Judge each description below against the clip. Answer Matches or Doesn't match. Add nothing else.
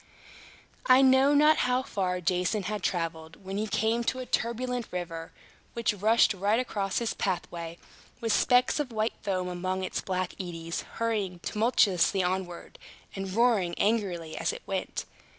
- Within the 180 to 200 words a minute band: Doesn't match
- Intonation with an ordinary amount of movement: Matches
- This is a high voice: Matches